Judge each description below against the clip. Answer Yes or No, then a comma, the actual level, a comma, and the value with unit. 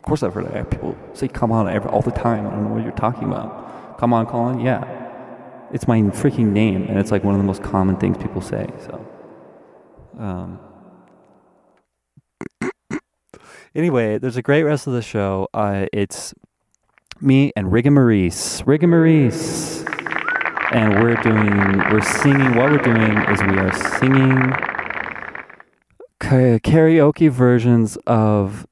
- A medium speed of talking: Yes, average, 145 wpm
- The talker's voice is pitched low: Yes, low, 115 Hz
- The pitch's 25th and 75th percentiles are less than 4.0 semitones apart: No, average, 4.4 semitones